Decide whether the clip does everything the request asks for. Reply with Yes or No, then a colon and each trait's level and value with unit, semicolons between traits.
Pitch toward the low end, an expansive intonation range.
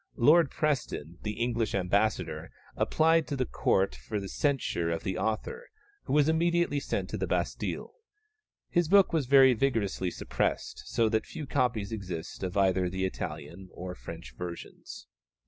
Yes: low, 110 Hz; wide, 7.5 semitones